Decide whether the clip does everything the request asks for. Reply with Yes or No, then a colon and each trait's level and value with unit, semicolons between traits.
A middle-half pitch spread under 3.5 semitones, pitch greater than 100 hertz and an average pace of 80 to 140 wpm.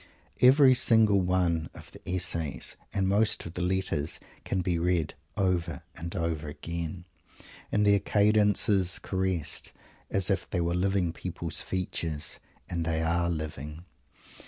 No: average, 2.8 semitones; very low, 90 Hz; slow, 135 wpm